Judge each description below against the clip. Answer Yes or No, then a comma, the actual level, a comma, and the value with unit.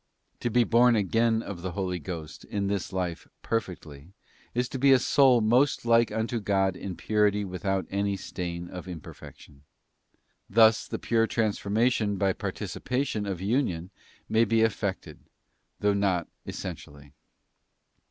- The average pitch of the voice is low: Yes, low, 100 Hz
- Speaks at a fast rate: No, average, 145 wpm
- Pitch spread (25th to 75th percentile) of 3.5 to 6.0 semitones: Yes, average, 3.8 semitones